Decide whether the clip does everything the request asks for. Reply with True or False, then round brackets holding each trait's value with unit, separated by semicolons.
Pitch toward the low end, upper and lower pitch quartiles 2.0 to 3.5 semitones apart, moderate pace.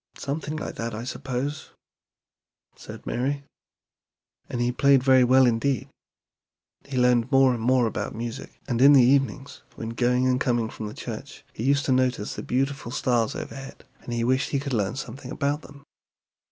True (130 Hz; 2.5 semitones; 170 wpm)